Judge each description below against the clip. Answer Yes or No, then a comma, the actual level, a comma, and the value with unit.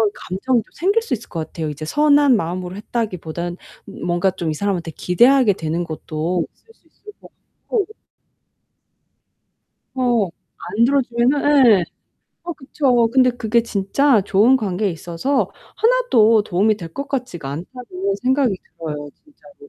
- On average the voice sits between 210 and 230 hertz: Yes, high, 220 Hz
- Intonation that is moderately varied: No, wide, 7.1 semitones